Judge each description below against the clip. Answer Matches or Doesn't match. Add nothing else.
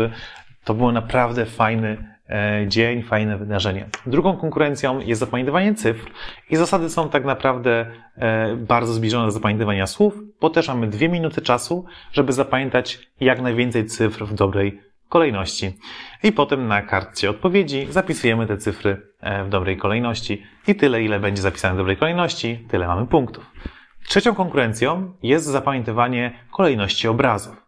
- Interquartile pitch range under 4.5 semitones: Doesn't match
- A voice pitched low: Matches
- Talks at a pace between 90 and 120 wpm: Doesn't match